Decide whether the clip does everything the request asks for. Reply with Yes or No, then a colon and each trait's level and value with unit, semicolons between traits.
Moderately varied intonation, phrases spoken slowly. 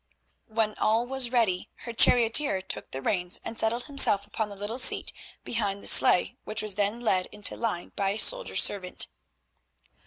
No: average, 3.0 semitones; average, 175 wpm